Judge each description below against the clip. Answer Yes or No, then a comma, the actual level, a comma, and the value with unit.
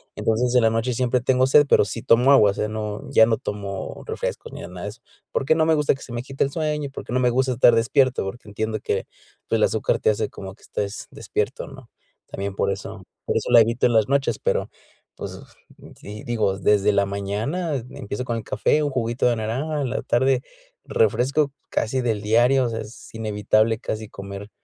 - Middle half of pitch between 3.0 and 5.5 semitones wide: Yes, average, 3.8 semitones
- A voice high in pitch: No, low, 115 Hz